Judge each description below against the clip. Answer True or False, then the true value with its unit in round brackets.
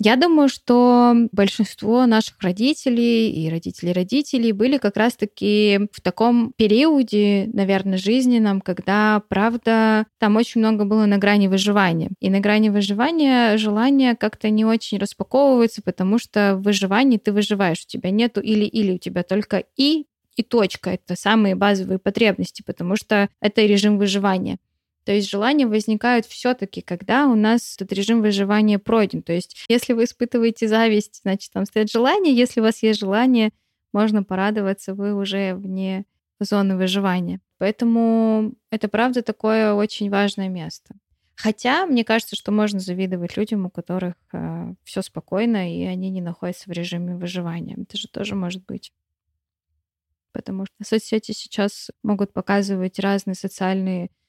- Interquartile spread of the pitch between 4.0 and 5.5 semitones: False (2.8 semitones)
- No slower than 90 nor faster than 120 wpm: False (145 wpm)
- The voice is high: True (210 Hz)